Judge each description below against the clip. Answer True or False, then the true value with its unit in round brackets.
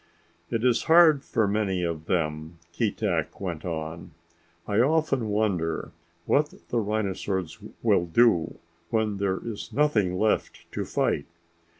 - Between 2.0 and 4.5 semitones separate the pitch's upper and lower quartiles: False (5.1 semitones)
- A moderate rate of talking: False (125 wpm)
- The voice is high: False (100 Hz)